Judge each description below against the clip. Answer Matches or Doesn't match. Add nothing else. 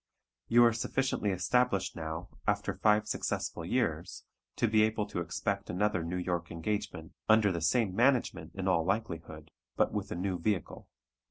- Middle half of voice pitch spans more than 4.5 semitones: Doesn't match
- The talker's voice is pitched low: Matches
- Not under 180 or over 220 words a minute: Doesn't match